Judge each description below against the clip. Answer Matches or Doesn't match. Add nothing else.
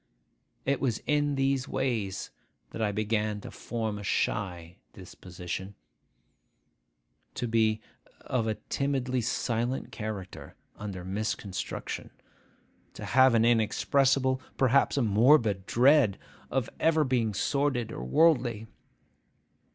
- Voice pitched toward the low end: Matches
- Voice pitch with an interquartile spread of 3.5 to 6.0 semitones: Matches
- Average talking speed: Doesn't match